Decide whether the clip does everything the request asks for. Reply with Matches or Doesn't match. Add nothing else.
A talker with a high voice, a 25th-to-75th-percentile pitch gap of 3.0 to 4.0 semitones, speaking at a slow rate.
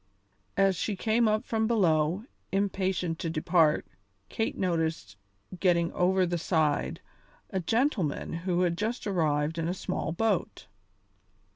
Doesn't match